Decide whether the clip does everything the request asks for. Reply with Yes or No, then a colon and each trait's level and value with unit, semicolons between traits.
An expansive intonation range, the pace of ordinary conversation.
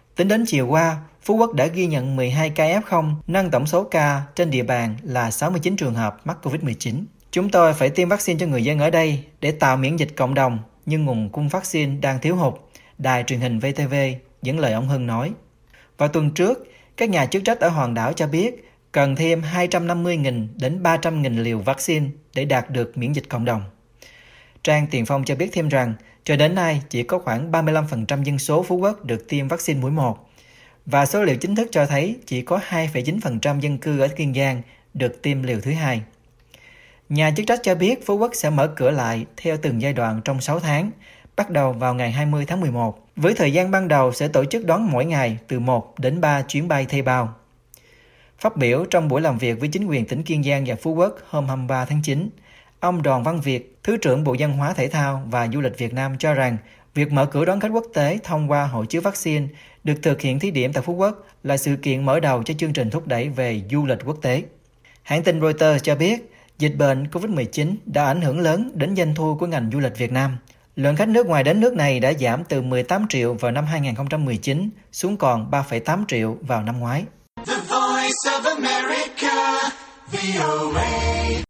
No: average, 4.5 semitones; average, 210 wpm